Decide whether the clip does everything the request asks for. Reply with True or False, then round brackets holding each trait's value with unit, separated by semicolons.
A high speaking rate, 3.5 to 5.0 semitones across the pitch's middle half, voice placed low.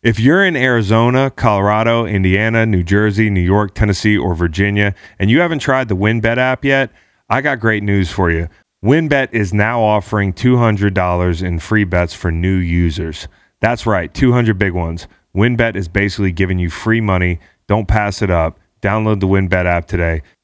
False (175 wpm; 3.8 semitones; 100 Hz)